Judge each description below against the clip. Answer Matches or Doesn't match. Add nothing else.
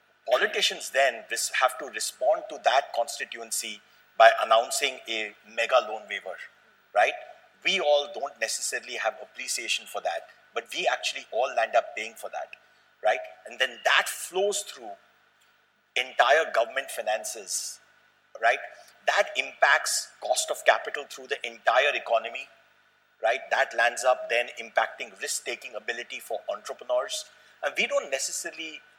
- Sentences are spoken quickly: Doesn't match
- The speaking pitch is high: Matches